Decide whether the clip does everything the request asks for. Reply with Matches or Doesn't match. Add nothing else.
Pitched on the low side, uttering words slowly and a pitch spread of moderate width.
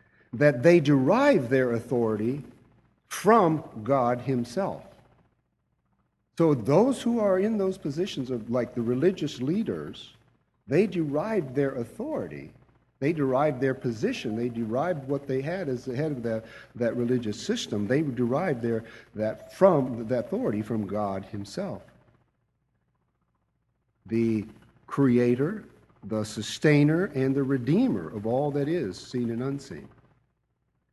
Matches